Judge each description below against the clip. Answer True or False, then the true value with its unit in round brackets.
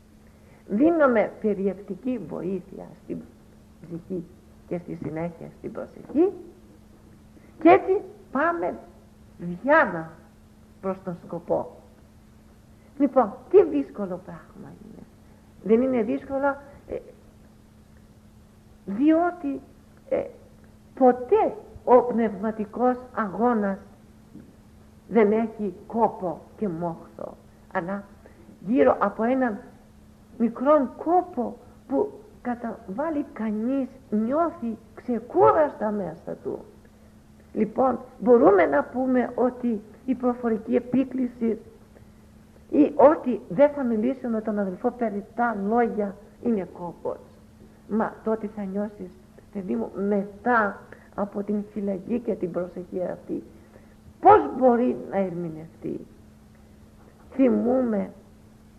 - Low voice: False (225 Hz)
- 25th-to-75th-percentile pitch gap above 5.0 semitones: False (4.6 semitones)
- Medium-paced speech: False (90 wpm)